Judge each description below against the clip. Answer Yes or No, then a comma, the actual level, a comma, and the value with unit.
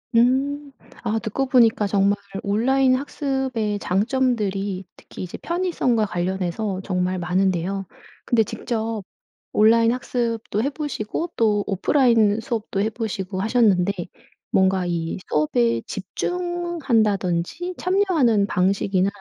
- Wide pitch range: No, average, 5.0 semitones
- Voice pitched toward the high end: Yes, high, 215 Hz